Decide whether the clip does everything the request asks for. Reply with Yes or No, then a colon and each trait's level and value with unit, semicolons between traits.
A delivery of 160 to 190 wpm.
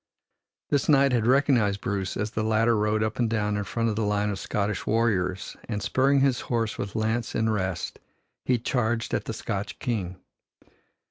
Yes: average, 185 wpm